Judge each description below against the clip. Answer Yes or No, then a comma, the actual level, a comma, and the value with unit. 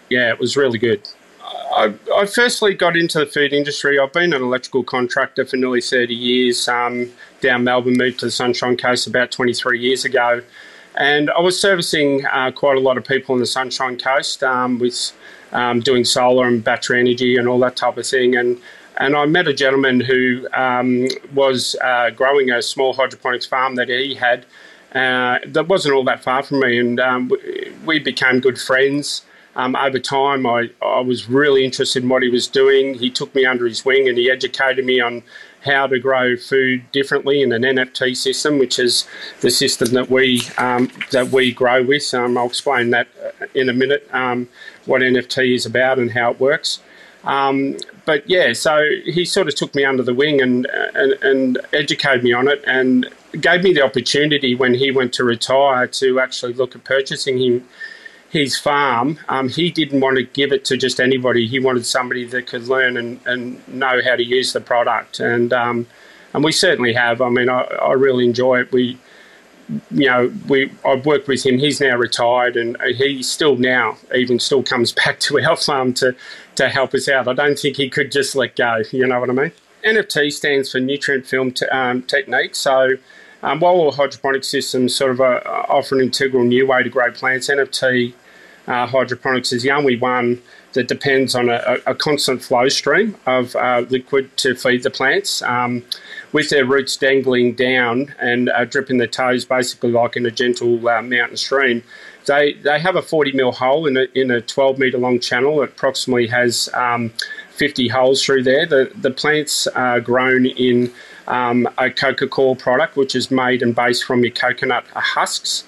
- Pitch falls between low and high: No, low, 130 Hz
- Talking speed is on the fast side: No, average, 195 wpm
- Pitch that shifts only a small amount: Yes, narrow, 1.9 semitones